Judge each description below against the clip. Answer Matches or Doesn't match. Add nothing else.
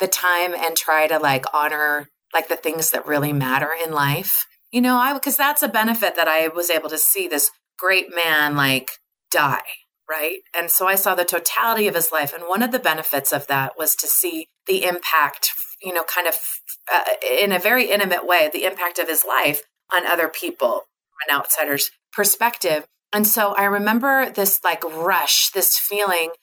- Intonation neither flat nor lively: Matches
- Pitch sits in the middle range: Matches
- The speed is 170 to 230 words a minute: Matches